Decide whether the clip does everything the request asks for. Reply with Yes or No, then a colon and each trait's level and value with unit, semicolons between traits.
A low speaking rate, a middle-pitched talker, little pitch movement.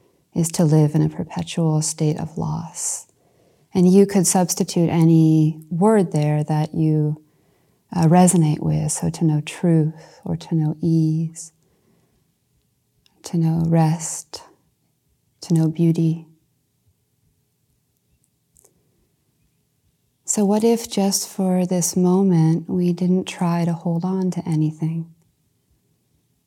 Yes: slow, 115 wpm; medium, 165 Hz; narrow, 2.3 semitones